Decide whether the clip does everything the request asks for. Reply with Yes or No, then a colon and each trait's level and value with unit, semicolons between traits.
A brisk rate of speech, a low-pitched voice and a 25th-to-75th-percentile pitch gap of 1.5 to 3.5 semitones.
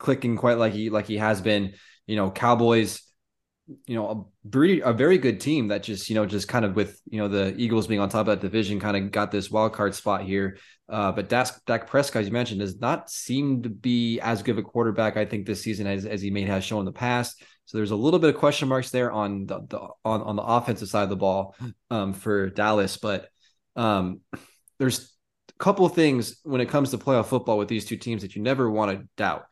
Yes: fast, 245 wpm; low, 110 Hz; average, 2.8 semitones